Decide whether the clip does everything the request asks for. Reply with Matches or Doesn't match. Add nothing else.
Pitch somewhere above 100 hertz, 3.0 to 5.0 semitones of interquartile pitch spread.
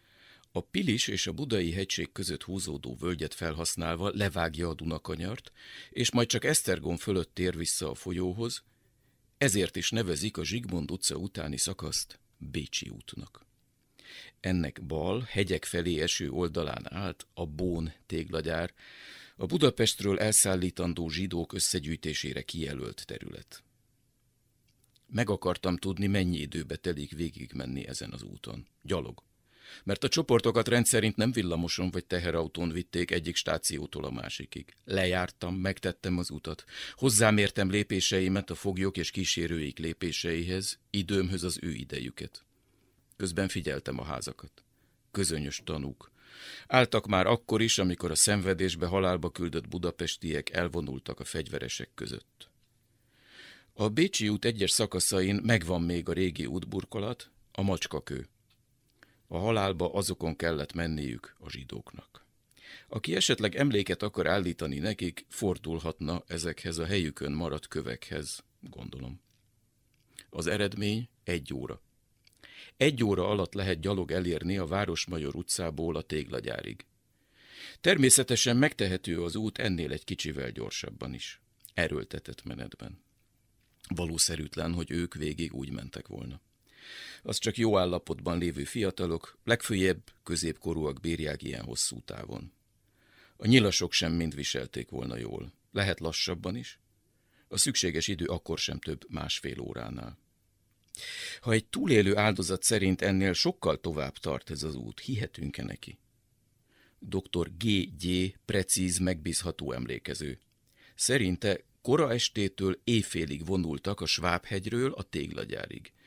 Doesn't match